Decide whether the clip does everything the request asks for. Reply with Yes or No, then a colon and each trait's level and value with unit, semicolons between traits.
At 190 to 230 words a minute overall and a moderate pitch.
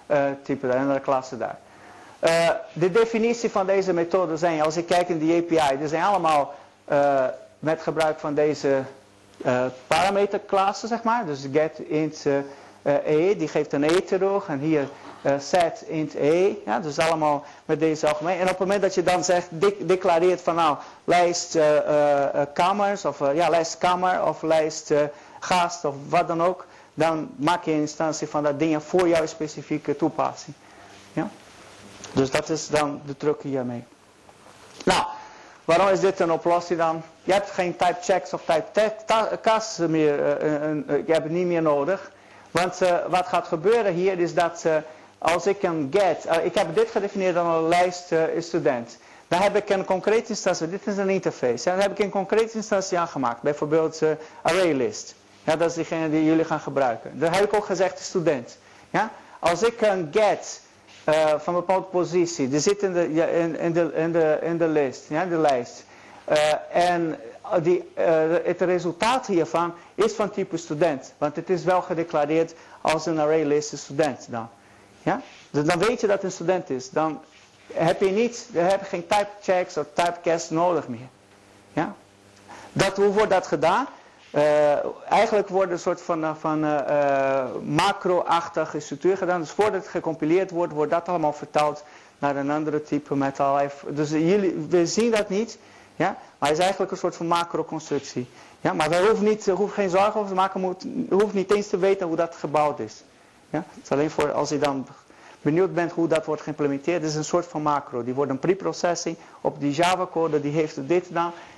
Yes: average, 195 wpm; medium, 165 Hz